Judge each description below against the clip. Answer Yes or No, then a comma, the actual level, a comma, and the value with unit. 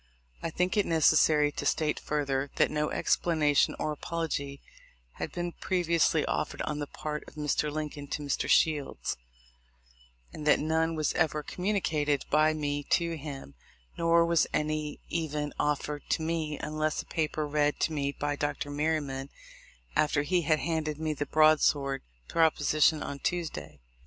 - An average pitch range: No, narrow, 1.7 semitones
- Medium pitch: Yes, medium, 150 Hz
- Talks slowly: No, average, 150 wpm